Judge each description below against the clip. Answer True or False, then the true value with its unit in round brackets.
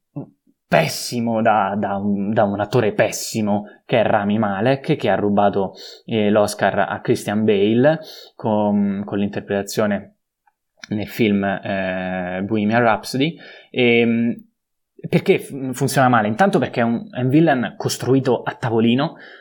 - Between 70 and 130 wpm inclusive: True (125 wpm)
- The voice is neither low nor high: False (110 Hz)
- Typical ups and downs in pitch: True (4.0 semitones)